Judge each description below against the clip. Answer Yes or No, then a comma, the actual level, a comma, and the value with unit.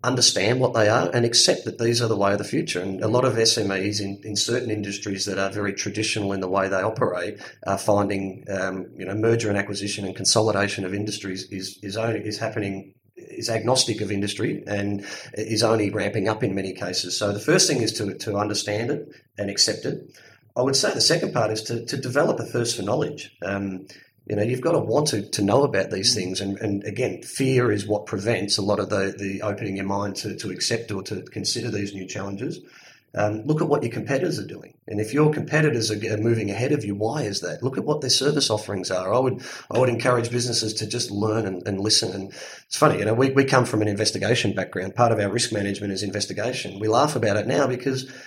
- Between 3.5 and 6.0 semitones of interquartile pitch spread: No, average, 2.9 semitones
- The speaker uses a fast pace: Yes, fast, 235 wpm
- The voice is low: Yes, low, 105 Hz